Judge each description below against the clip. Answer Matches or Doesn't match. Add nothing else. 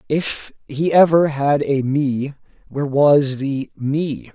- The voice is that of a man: Matches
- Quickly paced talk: Doesn't match